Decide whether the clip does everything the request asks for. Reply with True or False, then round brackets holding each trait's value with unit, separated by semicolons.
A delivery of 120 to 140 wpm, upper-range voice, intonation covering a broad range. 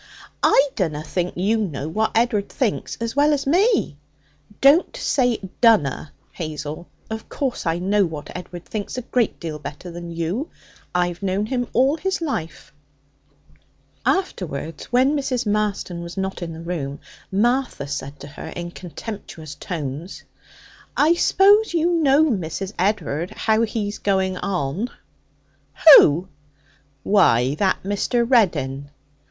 True (135 wpm; 195 Hz; 6.9 semitones)